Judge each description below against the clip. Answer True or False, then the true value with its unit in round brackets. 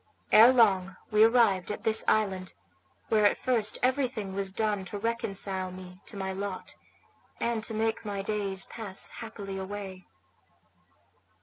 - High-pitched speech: True (205 Hz)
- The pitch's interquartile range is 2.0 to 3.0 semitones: True (2.6 semitones)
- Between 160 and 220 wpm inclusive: False (140 wpm)